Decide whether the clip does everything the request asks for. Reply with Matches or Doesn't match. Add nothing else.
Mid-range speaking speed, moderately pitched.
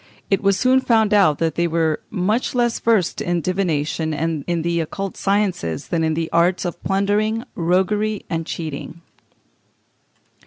Matches